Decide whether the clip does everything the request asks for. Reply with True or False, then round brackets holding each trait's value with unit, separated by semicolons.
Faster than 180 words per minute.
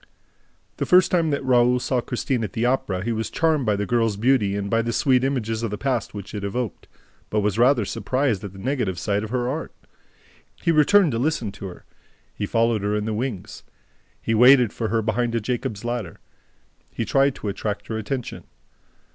True (205 wpm)